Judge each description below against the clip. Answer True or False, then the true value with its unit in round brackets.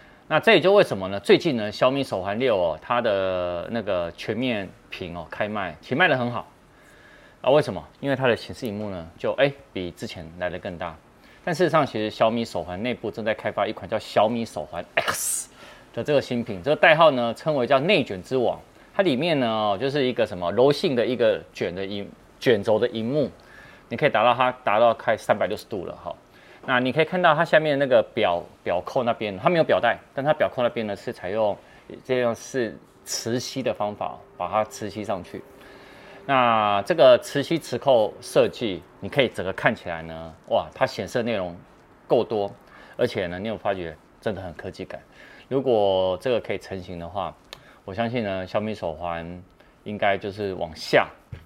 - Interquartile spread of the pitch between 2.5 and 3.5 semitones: False (5.4 semitones)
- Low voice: True (105 Hz)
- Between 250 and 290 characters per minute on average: True (285 characters per minute)